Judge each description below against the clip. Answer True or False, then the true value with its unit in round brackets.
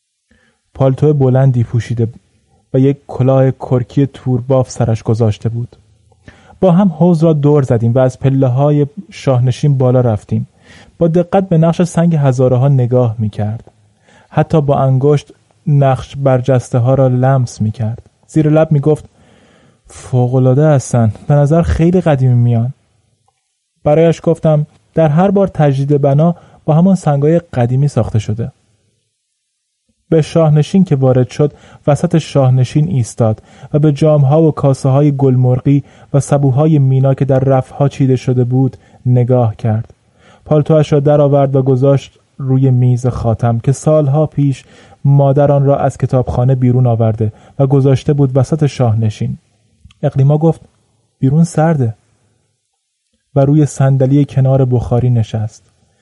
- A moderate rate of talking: True (135 wpm)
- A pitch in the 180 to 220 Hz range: False (135 Hz)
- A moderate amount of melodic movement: True (3.8 semitones)